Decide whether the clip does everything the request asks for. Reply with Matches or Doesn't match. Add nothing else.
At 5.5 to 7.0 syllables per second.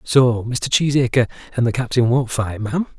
Doesn't match